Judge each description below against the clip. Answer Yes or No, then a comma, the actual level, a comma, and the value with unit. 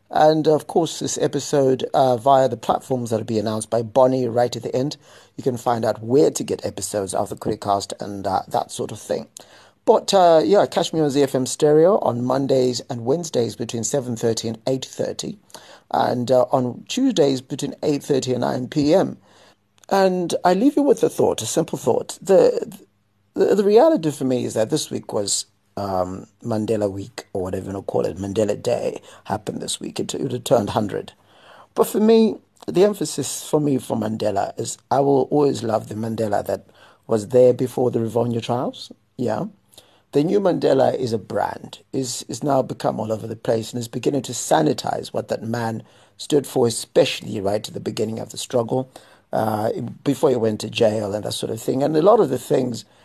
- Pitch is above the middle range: No, low, 125 Hz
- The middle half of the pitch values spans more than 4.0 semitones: Yes, average, 4.5 semitones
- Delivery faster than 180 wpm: Yes, average, 200 wpm